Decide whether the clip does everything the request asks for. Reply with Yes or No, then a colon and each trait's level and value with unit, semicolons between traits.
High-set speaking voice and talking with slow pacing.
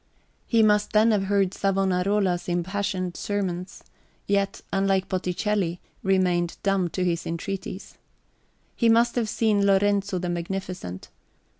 Yes: high, 195 Hz; slow, 120 wpm